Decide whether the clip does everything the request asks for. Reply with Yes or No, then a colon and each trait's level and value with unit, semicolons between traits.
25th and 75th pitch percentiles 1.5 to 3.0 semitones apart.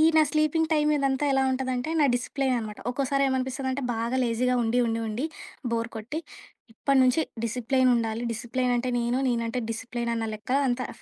Yes: narrow, 2.5 semitones